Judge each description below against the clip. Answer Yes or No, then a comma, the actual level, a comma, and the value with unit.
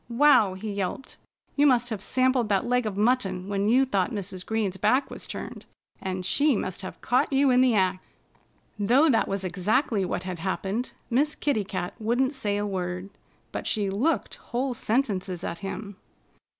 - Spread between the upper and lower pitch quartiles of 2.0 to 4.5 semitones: No, average, 4.9 semitones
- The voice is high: Yes, high, 210 Hz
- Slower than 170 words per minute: No, average, 175 wpm